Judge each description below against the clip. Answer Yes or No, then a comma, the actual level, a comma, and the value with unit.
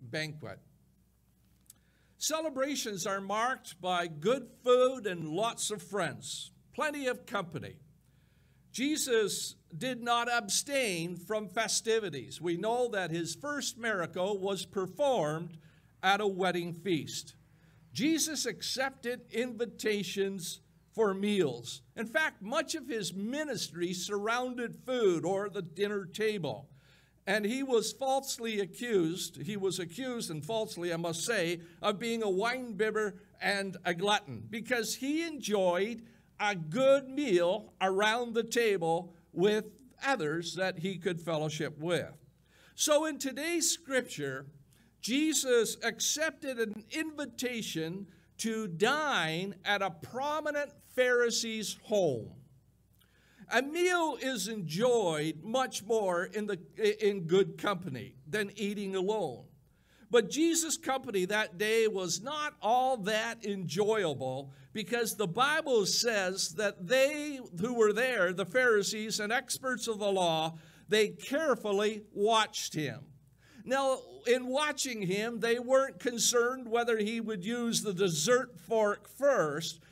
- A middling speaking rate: No, slow, 120 wpm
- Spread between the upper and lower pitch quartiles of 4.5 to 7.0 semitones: Yes, wide, 5.5 semitones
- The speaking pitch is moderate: No, high, 210 Hz